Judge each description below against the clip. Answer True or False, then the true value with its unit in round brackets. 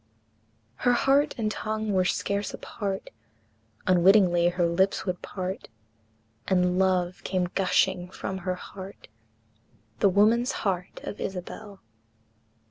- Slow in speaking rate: True (115 wpm)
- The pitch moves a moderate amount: False (2.0 semitones)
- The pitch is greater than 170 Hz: True (190 Hz)